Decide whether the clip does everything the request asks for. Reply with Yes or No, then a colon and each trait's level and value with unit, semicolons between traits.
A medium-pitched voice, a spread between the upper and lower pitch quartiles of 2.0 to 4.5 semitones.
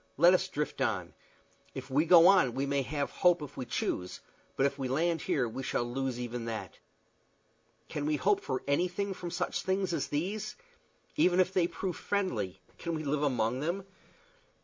No: medium, 150 Hz; wide, 5.5 semitones